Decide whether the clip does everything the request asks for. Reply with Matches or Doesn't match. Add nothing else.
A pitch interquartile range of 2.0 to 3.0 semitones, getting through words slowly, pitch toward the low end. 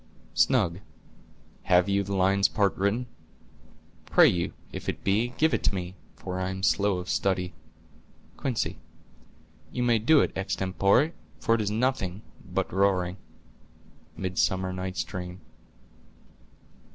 Matches